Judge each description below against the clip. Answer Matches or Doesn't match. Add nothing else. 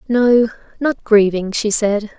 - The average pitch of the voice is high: Matches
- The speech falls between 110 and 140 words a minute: Matches